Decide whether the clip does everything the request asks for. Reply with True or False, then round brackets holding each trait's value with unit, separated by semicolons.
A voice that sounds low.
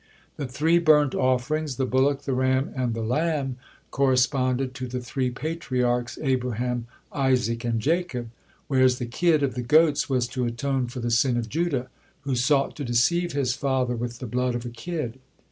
True (130 Hz)